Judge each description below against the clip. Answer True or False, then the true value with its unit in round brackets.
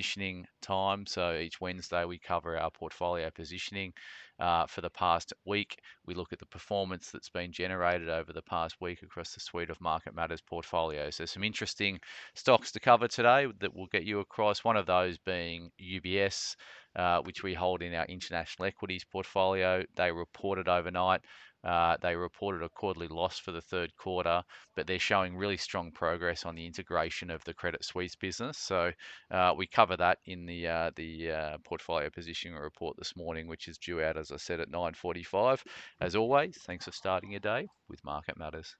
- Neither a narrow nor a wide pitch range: False (2.3 semitones)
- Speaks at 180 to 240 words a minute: True (185 wpm)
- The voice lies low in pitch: True (90 Hz)